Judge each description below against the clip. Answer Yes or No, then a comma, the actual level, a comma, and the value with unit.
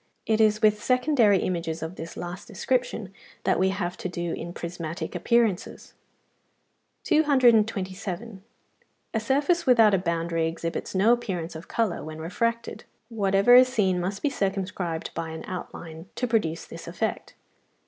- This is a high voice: Yes, high, 195 Hz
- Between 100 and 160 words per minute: Yes, average, 150 wpm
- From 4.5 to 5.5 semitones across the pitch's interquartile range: Yes, average, 5.1 semitones